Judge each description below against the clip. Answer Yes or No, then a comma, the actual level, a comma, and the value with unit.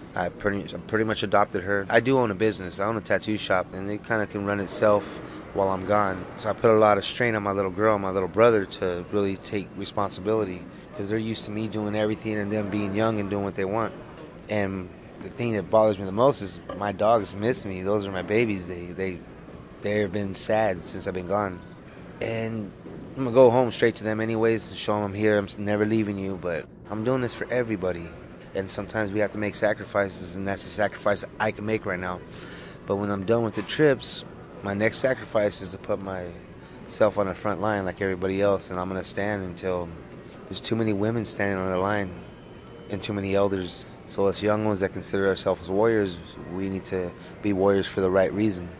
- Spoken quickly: Yes, fast, 225 wpm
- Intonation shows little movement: Yes, narrow, 2.2 semitones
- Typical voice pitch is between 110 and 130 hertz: No, low, 100 Hz